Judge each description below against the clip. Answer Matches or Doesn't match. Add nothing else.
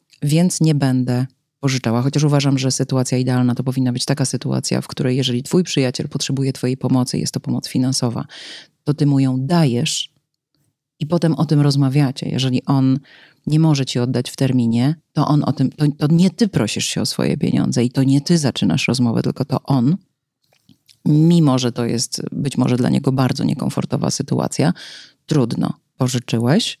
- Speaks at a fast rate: Matches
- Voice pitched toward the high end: Doesn't match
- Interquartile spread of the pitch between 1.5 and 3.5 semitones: Matches